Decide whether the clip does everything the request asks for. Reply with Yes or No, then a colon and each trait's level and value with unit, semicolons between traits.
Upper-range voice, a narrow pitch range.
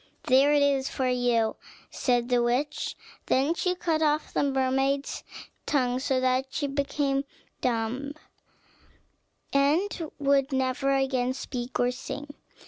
Yes: very high, 270 Hz; narrow, 2.1 semitones